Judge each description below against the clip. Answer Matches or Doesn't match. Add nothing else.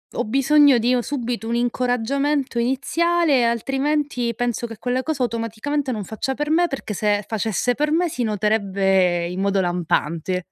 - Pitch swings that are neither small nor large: Matches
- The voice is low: Doesn't match